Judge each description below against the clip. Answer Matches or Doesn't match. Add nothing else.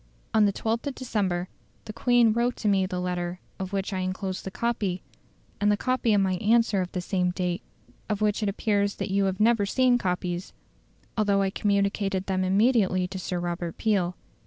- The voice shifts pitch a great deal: Doesn't match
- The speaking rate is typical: Matches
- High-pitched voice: Matches